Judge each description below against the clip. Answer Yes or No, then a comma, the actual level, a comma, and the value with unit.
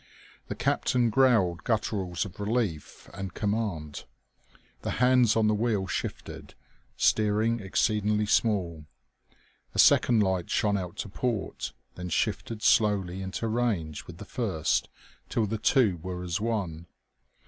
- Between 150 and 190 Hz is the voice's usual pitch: No, low, 105 Hz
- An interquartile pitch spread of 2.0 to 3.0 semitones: No, average, 3.8 semitones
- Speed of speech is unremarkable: No, slow, 130 wpm